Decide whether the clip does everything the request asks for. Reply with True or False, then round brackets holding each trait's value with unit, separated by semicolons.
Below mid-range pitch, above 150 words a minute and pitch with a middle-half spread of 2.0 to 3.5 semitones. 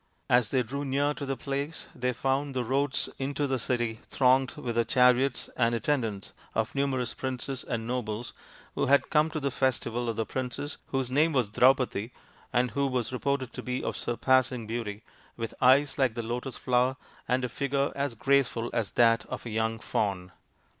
True (125 Hz; 185 wpm; 2.7 semitones)